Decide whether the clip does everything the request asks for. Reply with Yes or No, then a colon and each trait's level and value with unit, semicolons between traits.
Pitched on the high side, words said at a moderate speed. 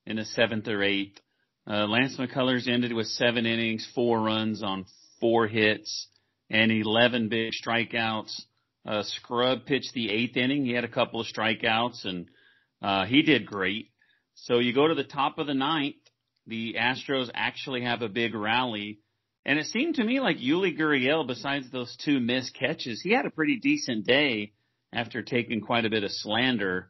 No: low, 120 Hz; average, 180 wpm